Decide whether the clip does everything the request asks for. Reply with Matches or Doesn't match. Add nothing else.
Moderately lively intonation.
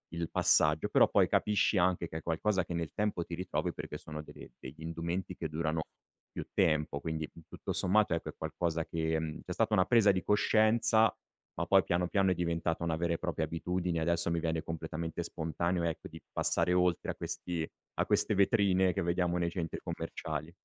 Doesn't match